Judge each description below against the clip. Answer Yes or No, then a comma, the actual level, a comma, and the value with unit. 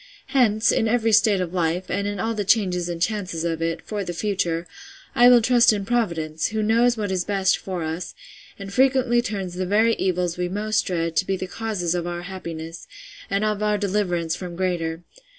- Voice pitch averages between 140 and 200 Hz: Yes, high, 190 Hz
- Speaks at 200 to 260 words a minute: Yes, fast, 205 wpm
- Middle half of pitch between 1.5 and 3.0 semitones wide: No, average, 3.7 semitones